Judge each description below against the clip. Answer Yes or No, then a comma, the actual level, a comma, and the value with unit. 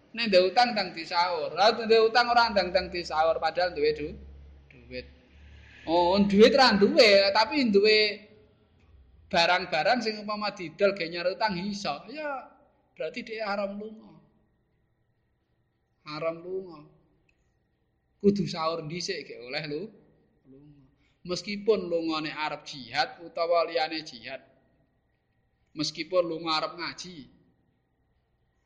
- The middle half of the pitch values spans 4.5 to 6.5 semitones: Yes, average, 5.2 semitones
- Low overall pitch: No, medium, 180 Hz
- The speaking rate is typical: Yes, average, 110 wpm